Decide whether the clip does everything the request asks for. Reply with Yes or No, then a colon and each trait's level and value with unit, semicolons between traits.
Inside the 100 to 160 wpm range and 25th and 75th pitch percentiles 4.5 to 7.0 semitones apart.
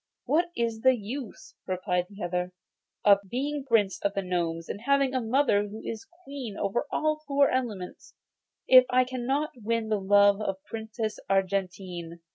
No: average, 170 wpm; average, 4.9 semitones